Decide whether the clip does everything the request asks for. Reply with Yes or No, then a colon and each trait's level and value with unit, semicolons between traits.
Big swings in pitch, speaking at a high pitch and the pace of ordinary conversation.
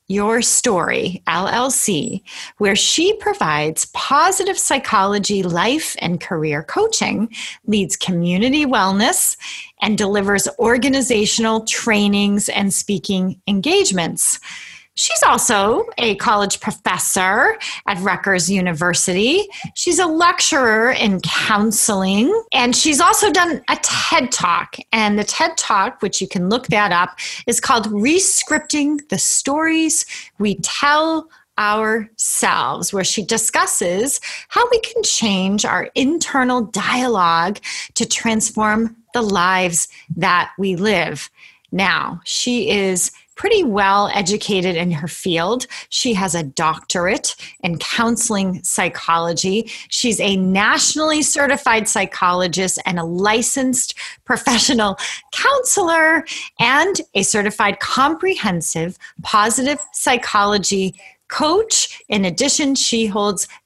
No: wide, 6.4 semitones; high, 220 Hz; slow, 105 wpm